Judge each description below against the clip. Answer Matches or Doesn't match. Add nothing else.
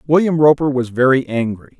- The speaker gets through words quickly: Doesn't match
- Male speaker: Matches